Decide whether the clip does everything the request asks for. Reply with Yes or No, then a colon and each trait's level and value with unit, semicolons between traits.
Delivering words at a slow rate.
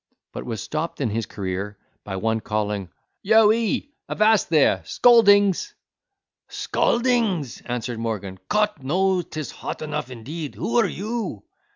Yes: slow, 130 wpm